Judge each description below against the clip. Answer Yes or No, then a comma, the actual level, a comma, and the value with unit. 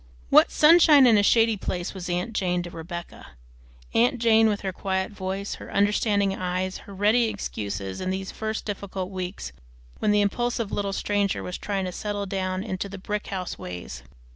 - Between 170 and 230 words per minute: Yes, average, 180 wpm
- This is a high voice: Yes, high, 195 Hz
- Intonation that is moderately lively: No, narrow, 2.2 semitones